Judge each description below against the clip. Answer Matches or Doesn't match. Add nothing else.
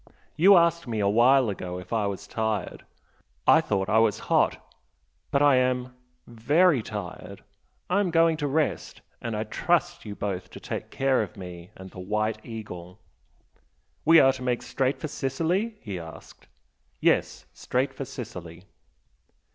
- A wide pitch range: Matches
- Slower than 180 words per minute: Matches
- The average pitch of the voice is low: Matches